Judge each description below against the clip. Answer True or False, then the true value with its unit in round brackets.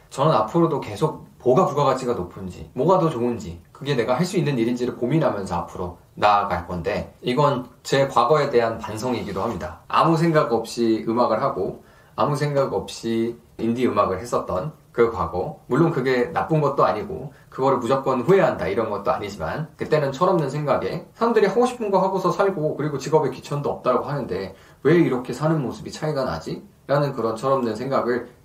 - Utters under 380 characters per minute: False (390 characters per minute)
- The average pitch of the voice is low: True (130 Hz)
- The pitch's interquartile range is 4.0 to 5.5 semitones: True (5.2 semitones)